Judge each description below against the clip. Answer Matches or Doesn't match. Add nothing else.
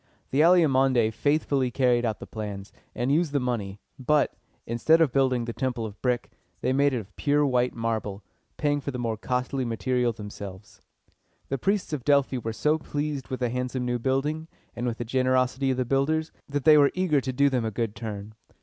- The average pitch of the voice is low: Matches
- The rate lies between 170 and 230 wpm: Matches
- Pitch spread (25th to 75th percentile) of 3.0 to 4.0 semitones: Matches